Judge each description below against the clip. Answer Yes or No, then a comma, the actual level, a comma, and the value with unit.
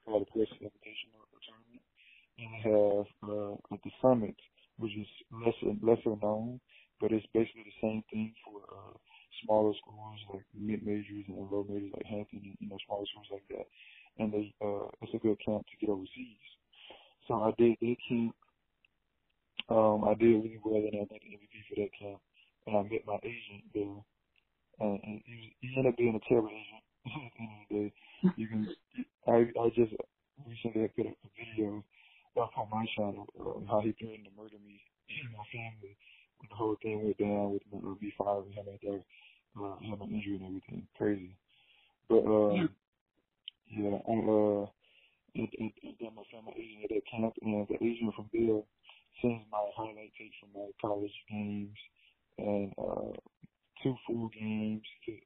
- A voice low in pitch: Yes, low, 105 Hz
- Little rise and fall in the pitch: Yes, narrow, 1.6 semitones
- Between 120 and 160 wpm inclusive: No, average, 180 wpm